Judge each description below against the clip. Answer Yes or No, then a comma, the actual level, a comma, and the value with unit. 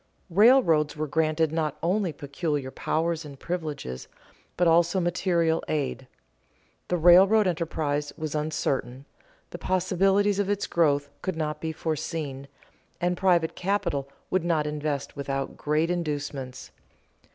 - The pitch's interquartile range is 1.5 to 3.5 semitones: Yes, average, 3.2 semitones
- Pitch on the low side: No, medium, 160 Hz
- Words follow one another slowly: Yes, slow, 130 wpm